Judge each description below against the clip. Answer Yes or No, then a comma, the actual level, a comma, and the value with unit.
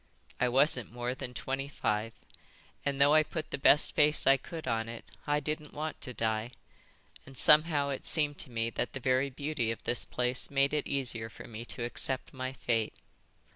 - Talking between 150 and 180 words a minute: No, average, 195 wpm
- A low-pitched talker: Yes, low, 130 Hz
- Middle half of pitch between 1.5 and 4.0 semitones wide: Yes, average, 3.4 semitones